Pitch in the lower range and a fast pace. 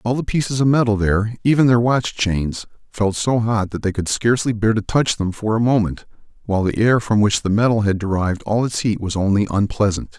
Yes: low, 110 Hz; fast, 230 wpm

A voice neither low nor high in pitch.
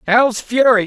No: high, 230 Hz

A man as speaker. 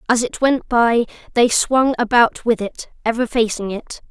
No: female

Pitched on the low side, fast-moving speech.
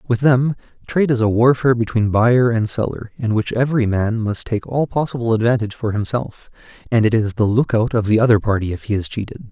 Yes: low, 115 Hz; fast, 215 wpm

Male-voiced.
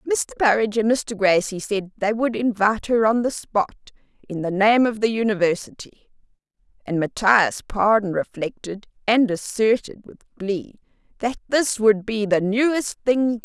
No: female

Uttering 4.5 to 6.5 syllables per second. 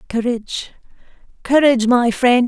Yes: 4.9 syllables/s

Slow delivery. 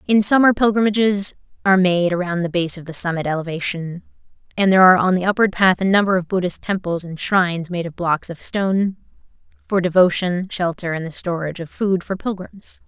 No: average, 190 wpm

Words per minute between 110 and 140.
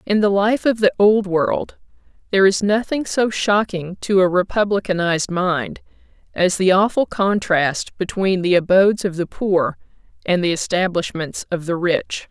No: average, 155 wpm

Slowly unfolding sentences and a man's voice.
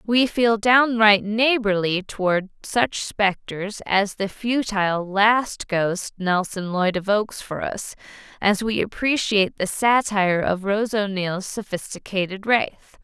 No: slow, 125 wpm; female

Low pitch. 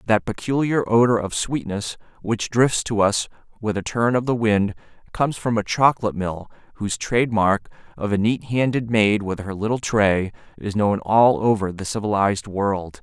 Yes: low, 110 Hz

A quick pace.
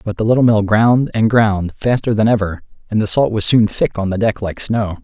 Yes: fast, 250 wpm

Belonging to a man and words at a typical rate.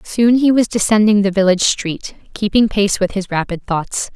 No: female; average, 190 wpm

